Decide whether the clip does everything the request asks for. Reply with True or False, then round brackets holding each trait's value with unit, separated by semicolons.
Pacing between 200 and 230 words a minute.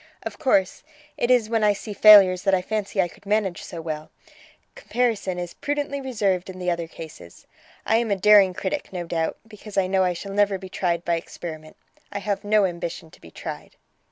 True (205 wpm)